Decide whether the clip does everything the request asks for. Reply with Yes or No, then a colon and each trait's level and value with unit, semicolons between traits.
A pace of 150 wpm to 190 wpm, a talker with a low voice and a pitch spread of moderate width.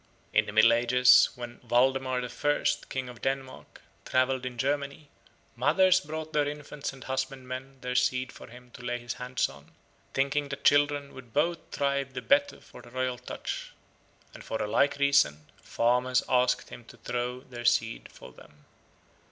No: average, 170 wpm; low, 130 Hz; narrow, 2.2 semitones